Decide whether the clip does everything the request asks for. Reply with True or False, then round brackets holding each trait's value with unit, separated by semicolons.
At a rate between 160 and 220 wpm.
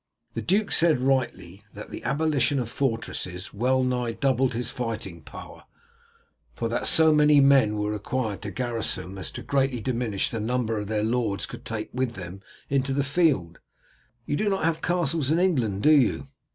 True (180 wpm)